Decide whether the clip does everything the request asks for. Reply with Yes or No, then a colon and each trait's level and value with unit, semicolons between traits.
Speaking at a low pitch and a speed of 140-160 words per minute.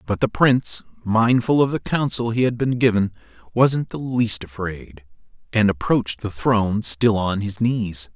No: low, 110 Hz; average, 170 wpm